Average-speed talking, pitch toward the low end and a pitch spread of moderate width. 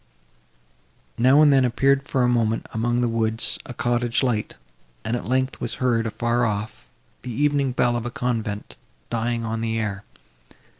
No: average, 165 wpm; low, 120 Hz; narrow, 2.1 semitones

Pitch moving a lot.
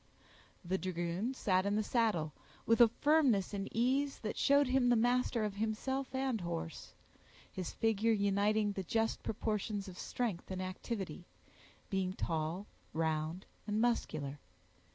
No: average, 4.2 semitones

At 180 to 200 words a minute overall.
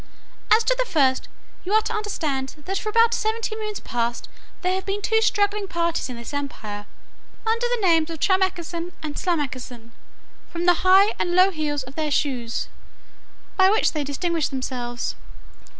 No: average, 165 wpm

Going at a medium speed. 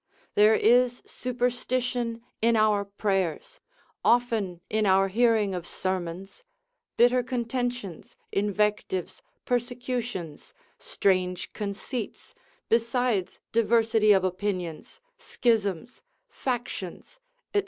No: slow, 85 wpm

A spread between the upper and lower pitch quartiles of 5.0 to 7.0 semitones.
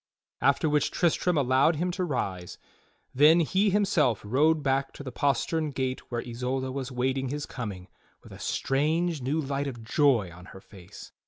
No: average, 3.8 semitones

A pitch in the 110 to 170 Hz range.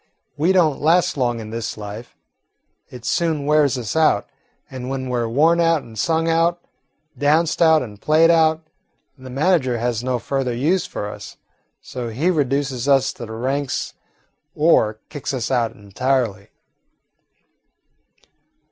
Yes: low, 135 Hz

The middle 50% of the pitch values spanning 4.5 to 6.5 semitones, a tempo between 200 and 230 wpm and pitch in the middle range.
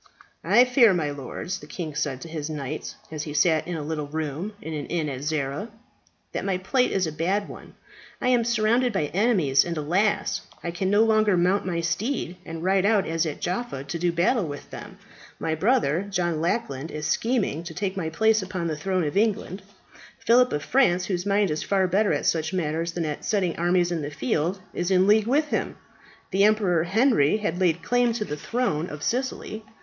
Yes: average, 4.9 semitones; fast, 205 wpm; medium, 175 Hz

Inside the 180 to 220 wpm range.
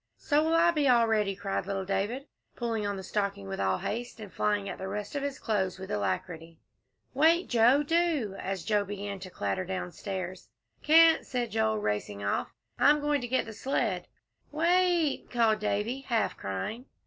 Yes: average, 185 wpm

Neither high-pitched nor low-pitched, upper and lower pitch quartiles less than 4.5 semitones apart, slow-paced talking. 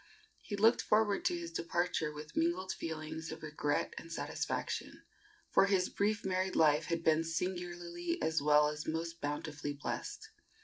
No: medium, 165 Hz; narrow, 2.6 semitones; average, 150 wpm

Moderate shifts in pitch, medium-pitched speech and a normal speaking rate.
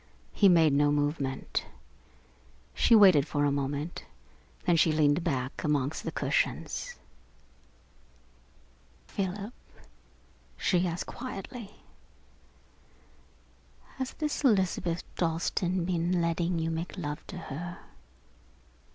No: average, 4.2 semitones; medium, 170 Hz; slow, 100 wpm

